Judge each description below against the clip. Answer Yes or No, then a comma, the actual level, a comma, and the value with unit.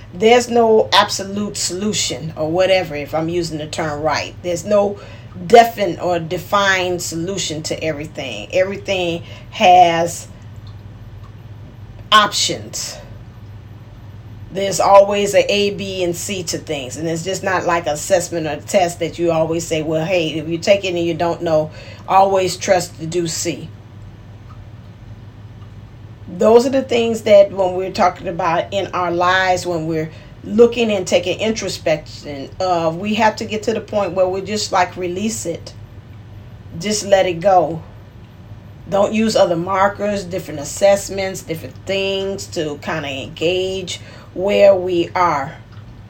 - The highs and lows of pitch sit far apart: Yes, wide, 8.2 semitones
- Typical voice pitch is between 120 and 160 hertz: No, medium, 170 Hz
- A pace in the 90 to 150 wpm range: Yes, average, 145 wpm